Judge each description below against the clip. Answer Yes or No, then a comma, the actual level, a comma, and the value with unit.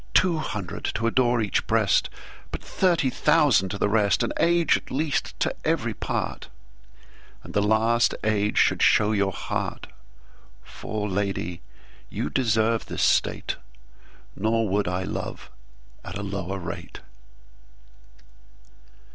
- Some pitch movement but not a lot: Yes, average, 4.2 semitones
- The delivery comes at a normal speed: No, slow, 110 wpm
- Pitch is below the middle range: Yes, low, 105 Hz